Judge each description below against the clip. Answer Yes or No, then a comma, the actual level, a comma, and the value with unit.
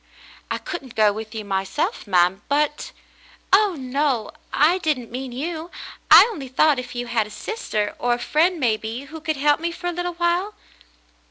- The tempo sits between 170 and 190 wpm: No, average, 200 wpm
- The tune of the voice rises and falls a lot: Yes, wide, 6.7 semitones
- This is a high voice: Yes, very high, 280 Hz